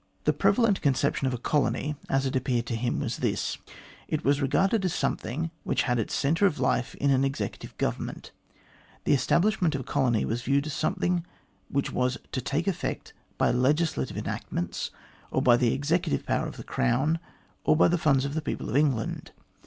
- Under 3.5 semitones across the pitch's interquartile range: No, average, 3.8 semitones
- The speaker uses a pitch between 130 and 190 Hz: Yes, medium, 140 Hz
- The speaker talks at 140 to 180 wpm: No, average, 190 wpm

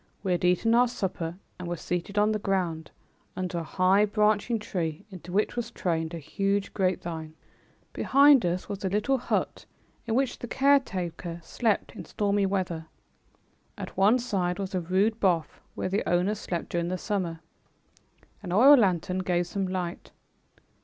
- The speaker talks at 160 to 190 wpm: Yes, average, 165 wpm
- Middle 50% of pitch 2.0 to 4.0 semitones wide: Yes, average, 3.2 semitones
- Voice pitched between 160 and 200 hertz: Yes, high, 190 Hz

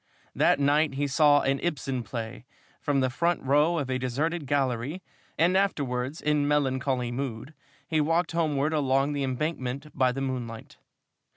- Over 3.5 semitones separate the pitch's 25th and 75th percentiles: No, average, 2.8 semitones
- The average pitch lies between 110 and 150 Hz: Yes, medium, 140 Hz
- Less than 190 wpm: Yes, average, 155 wpm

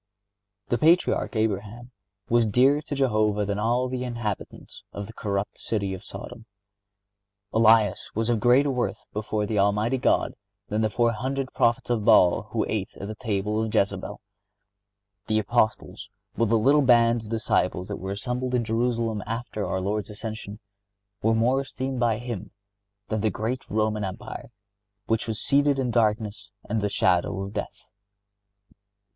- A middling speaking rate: Yes, average, 155 wpm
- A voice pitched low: Yes, low, 110 Hz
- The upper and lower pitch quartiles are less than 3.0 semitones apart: Yes, narrow, 2.6 semitones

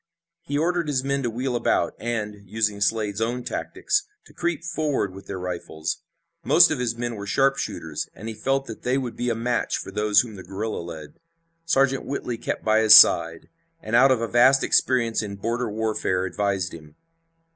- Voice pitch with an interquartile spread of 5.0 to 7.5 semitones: No, average, 4.4 semitones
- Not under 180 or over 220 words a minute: Yes, average, 190 wpm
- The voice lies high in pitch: No, low, 115 Hz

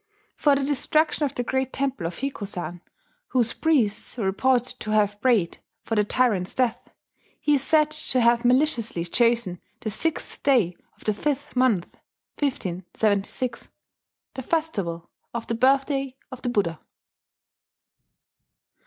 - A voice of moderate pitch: No, high, 245 Hz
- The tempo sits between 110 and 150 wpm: Yes, slow, 135 wpm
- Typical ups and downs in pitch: Yes, average, 4.9 semitones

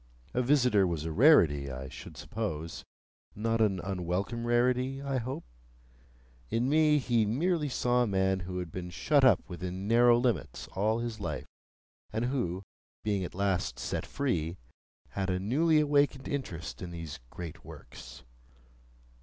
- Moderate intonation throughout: No, wide, 6.1 semitones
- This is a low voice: Yes, low, 110 Hz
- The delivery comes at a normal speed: Yes, average, 150 wpm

